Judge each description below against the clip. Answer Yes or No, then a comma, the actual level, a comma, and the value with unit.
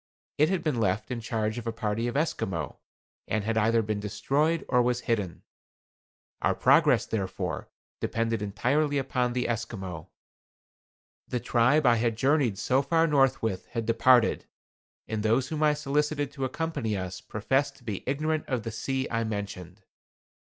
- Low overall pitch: Yes, low, 120 Hz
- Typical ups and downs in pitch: Yes, average, 4.2 semitones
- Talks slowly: No, average, 160 wpm